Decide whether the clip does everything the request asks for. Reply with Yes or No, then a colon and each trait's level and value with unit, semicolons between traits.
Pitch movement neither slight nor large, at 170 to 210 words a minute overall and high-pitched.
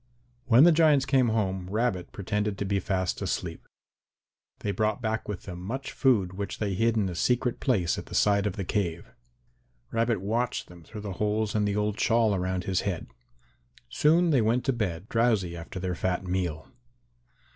No: average, 3.8 semitones; average, 185 wpm; low, 105 Hz